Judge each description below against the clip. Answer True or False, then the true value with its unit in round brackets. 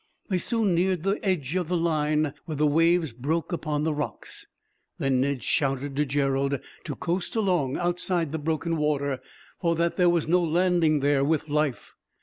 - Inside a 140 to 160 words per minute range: False (175 wpm)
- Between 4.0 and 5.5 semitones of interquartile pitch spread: False (3.4 semitones)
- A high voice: False (155 Hz)